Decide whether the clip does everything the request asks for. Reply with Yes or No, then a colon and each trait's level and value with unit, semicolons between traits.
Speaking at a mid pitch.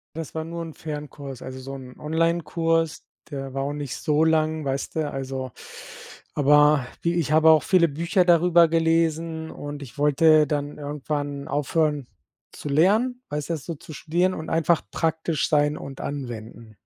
Yes: medium, 150 Hz